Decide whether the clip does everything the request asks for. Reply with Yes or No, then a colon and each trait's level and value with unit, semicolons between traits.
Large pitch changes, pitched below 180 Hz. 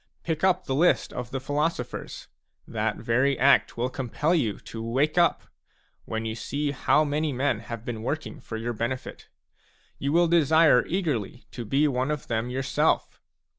No: average, 4.2 semitones; low, 135 Hz